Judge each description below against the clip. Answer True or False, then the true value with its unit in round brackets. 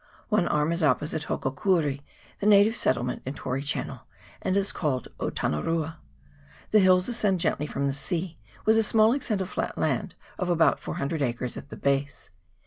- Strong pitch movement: True (5.8 semitones)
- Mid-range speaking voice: True (165 Hz)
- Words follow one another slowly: False (175 wpm)